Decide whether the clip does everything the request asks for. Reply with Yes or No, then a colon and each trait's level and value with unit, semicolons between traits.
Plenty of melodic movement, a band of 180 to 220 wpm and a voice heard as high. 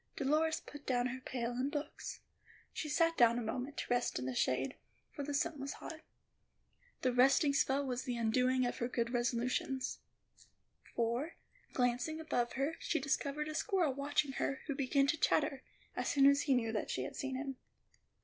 No: average, 2.9 semitones; average, 185 wpm; very high, 270 Hz